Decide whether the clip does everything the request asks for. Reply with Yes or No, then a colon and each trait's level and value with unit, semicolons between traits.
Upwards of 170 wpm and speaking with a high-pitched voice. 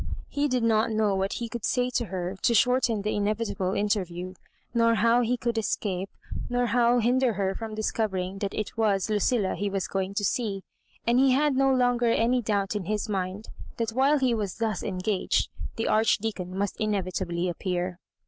Yes: average, 185 wpm; high, 215 Hz